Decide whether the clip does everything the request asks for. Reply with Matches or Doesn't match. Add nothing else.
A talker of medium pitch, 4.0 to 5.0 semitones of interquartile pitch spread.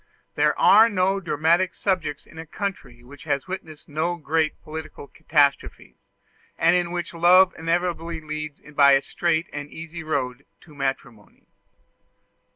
Doesn't match